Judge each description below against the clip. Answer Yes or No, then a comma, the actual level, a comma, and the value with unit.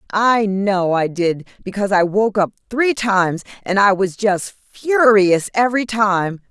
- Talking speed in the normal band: Yes, average, 155 wpm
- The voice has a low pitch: No, high, 200 Hz